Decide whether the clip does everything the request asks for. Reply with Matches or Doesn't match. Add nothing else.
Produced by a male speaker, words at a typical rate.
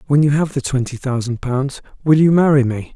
Doesn't match